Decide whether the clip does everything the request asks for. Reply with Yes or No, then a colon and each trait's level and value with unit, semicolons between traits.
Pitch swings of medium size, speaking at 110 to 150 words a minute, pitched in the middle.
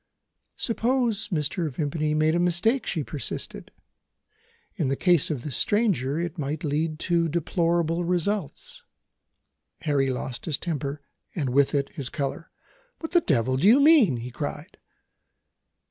Yes: average, 4.3 semitones; average, 145 wpm; medium, 160 Hz